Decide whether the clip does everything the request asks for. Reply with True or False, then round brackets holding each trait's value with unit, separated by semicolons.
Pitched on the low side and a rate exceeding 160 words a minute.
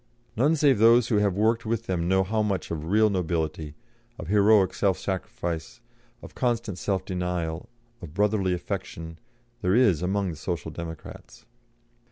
False (95 Hz; 155 wpm)